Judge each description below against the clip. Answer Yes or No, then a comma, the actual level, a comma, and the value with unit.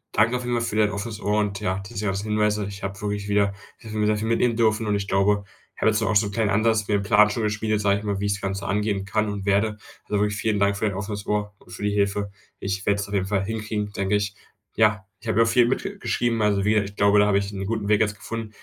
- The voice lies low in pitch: Yes, low, 105 Hz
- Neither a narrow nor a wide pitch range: No, narrow, 1.3 semitones